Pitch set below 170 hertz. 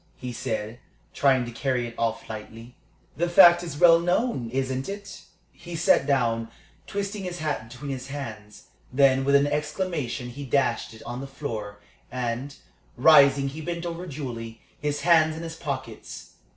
Yes: medium, 140 Hz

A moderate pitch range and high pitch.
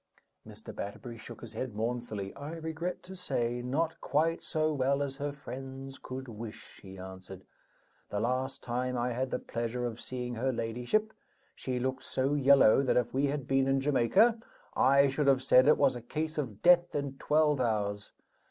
No: average, 3.2 semitones; low, 130 Hz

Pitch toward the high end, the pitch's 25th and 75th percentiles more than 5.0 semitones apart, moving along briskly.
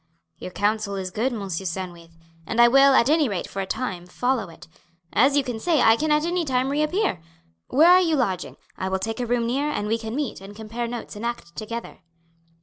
Yes: high, 235 Hz; wide, 5.6 semitones; fast, 210 wpm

